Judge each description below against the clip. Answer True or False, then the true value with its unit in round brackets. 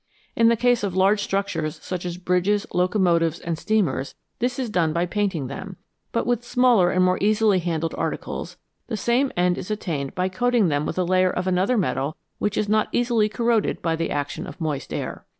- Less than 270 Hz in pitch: True (185 Hz)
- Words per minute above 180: True (200 wpm)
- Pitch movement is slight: False (4.1 semitones)